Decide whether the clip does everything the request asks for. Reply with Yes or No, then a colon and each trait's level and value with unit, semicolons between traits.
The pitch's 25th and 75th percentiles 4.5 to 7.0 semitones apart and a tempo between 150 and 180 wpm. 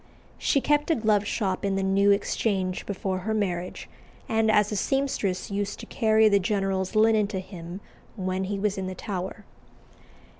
No: narrow, 2.4 semitones; average, 175 wpm